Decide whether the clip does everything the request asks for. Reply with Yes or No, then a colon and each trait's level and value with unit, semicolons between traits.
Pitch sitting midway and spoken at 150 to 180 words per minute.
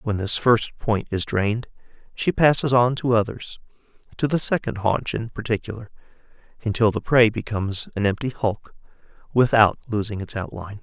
No: low, 115 Hz; average, 155 wpm